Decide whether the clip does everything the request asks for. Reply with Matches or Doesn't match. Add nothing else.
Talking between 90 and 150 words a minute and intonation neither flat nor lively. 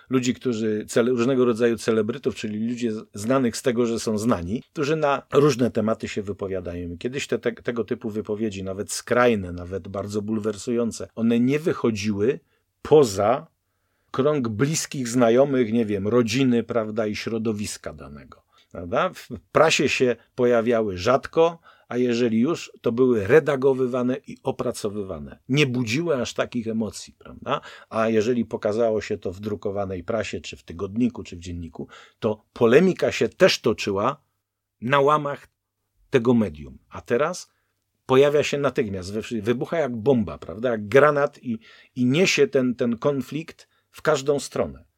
Matches